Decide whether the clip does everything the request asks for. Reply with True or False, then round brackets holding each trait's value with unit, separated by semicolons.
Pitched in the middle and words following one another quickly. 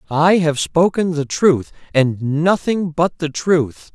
False (160 Hz; 150 wpm)